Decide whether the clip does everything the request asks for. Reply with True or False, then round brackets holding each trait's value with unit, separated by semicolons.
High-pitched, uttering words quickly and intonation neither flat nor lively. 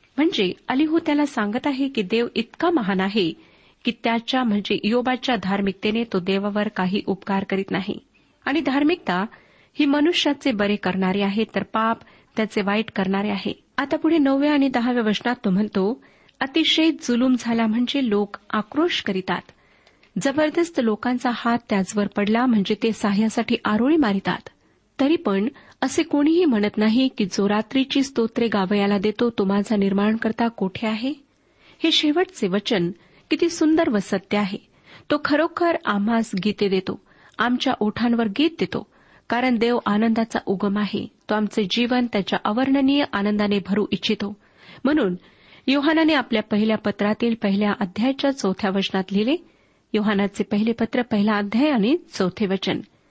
True (225 Hz; 140 wpm; 4.8 semitones)